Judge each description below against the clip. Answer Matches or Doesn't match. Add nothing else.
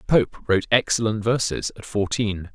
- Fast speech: Doesn't match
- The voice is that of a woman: Doesn't match